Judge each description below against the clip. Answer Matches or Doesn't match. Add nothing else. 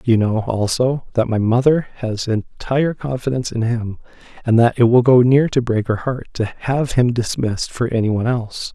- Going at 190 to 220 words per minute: Matches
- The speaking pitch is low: Matches